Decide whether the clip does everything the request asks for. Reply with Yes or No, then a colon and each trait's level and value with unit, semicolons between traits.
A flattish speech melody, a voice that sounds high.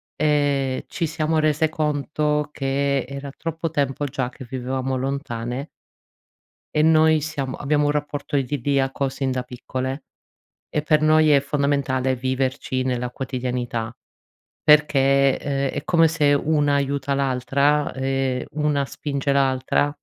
No: narrow, 2.2 semitones; medium, 140 Hz